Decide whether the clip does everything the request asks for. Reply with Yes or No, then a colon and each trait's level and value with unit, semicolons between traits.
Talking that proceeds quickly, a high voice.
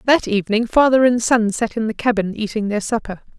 Yes: fast, 215 wpm; high, 225 Hz